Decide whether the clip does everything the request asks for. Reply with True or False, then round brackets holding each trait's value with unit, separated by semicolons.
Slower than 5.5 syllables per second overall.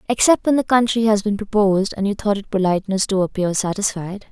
False (6.1 syllables/s)